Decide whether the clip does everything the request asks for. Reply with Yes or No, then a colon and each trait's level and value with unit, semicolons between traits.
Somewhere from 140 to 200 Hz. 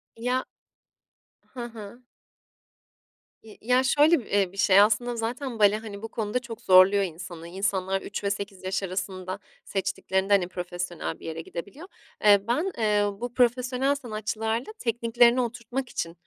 No: high, 215 Hz